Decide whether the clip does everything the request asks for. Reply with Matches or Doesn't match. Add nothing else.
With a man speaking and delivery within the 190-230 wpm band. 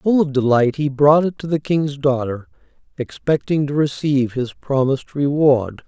Doesn't match